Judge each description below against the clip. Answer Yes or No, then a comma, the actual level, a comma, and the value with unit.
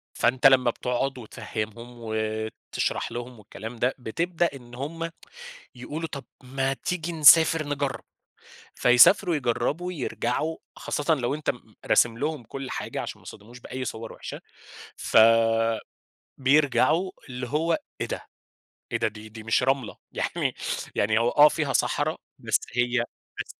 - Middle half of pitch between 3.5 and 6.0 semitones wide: Yes, average, 4.2 semitones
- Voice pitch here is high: No, low, 130 Hz